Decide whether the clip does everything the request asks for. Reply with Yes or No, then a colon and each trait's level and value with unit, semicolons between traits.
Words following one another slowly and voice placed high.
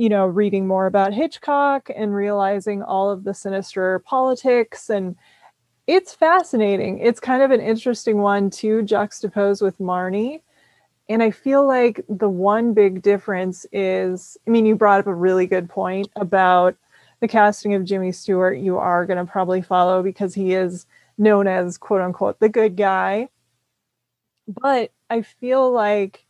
No: average, 155 wpm; high, 200 Hz